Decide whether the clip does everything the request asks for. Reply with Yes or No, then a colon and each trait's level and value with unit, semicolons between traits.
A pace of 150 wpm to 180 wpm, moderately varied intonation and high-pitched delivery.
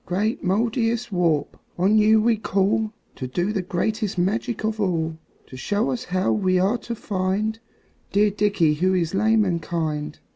Yes: average, 160 wpm; average, 3.5 semitones; high, 200 Hz